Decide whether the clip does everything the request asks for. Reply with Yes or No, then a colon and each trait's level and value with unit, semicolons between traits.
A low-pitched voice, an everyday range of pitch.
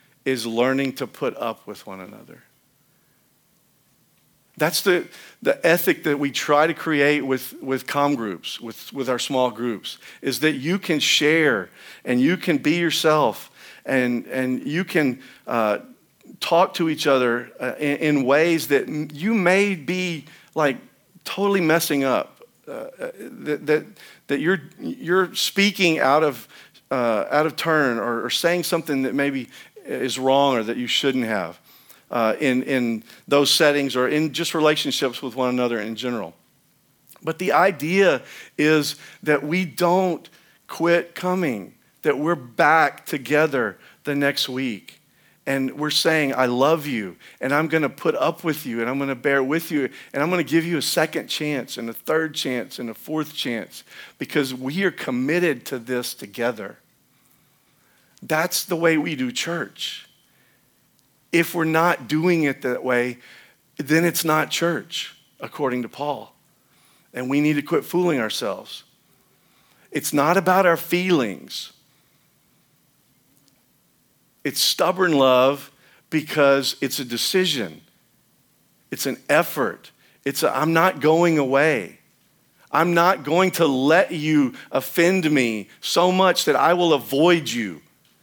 No: medium, 150 Hz; average, 4.2 semitones